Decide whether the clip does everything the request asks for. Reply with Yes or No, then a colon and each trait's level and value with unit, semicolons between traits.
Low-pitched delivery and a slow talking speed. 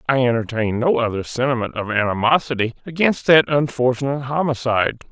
Yes: low, 130 Hz; slow, 130 wpm